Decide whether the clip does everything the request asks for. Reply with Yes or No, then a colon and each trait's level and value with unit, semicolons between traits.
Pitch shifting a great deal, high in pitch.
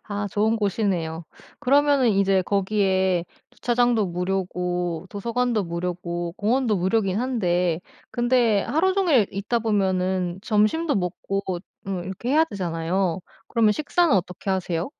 No: average, 4.5 semitones; high, 195 Hz